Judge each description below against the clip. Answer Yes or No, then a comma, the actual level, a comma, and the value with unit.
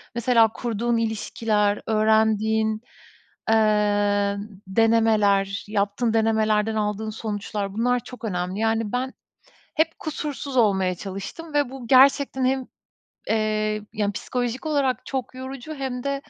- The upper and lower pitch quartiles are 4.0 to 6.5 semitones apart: No, average, 3.2 semitones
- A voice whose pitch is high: Yes, high, 225 Hz